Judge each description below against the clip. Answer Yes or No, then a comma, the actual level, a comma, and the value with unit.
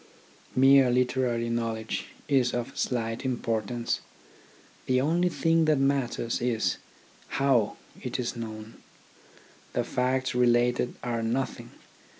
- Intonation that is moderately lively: No, narrow, 2.2 semitones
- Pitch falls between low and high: No, low, 125 Hz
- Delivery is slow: Yes, slow, 110 wpm